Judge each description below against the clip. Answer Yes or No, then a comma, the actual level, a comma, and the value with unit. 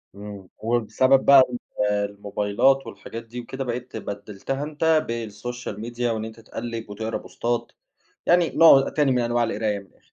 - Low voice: Yes, low, 115 Hz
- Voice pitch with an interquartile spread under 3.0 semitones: No, average, 3.3 semitones